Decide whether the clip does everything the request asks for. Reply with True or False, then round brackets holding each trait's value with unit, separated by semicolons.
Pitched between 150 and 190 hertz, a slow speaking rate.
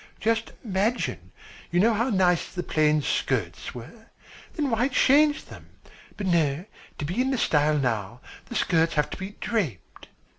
False (185 Hz; 155 wpm)